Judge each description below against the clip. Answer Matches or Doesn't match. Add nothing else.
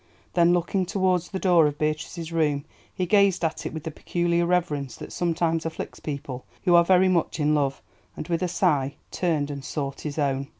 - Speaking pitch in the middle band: Matches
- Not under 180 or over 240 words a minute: Matches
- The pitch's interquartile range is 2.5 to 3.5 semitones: Matches